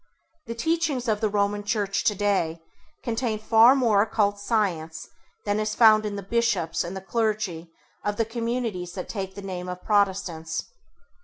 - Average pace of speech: Yes, average, 160 wpm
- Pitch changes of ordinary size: Yes, average, 3.0 semitones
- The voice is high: Yes, high, 205 Hz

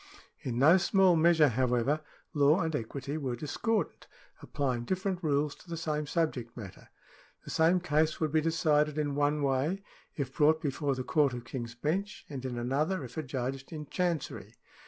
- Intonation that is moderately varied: Yes, average, 3.5 semitones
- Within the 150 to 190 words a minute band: Yes, average, 170 wpm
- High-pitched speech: No, medium, 150 Hz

